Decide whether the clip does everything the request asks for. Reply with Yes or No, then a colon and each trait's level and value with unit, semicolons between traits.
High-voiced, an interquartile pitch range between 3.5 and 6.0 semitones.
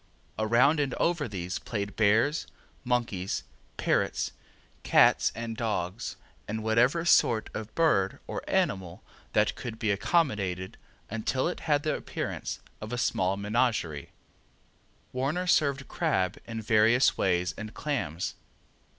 No: low, 115 Hz; average, 5.3 semitones